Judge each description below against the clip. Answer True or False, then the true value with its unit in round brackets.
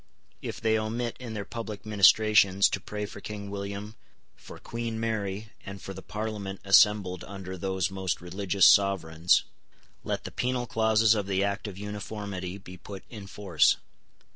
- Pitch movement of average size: False (2.0 semitones)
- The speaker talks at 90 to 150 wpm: False (160 wpm)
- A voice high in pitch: False (100 Hz)